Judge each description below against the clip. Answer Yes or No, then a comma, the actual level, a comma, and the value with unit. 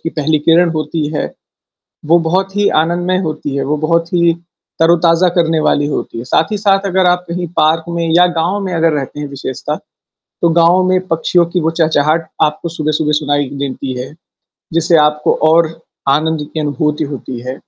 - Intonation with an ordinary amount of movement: No, narrow, 2.3 semitones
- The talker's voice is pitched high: No, medium, 160 Hz